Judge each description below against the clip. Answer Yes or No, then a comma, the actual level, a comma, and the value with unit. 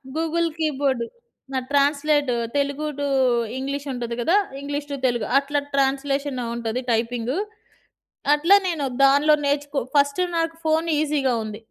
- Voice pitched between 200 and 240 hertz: No, very high, 280 Hz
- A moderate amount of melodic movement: No, narrow, 2.3 semitones